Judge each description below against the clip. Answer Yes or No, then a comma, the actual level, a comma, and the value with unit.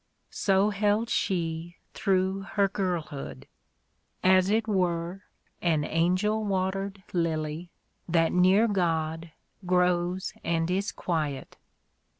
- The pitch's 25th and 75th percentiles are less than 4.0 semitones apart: Yes, average, 2.8 semitones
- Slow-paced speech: Yes, slow, 100 wpm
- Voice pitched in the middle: Yes, medium, 180 Hz